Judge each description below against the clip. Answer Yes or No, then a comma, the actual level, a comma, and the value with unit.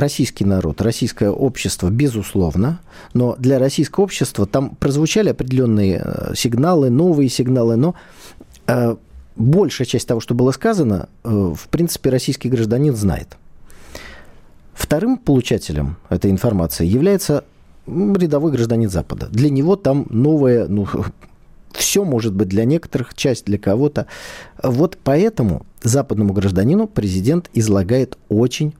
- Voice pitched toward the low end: Yes, low, 125 Hz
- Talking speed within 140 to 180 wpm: No, average, 120 wpm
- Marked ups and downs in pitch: Yes, wide, 6.0 semitones